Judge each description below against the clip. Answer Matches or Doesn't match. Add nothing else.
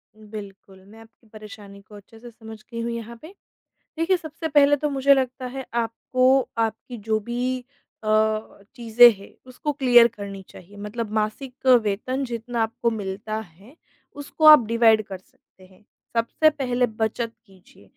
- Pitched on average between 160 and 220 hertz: Doesn't match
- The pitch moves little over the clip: Doesn't match